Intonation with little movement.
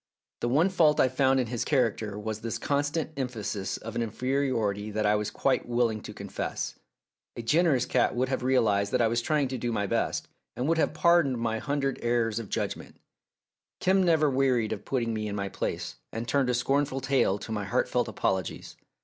No: average, 4.0 semitones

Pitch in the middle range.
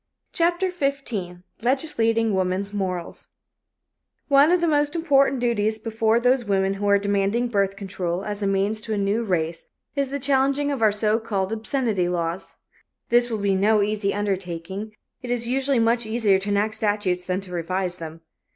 No: high, 210 Hz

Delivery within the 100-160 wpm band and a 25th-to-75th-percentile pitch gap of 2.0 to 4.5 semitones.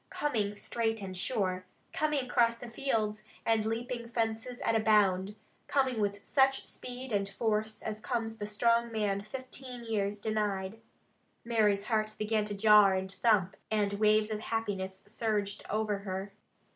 Yes: average, 150 wpm; narrow, 2.4 semitones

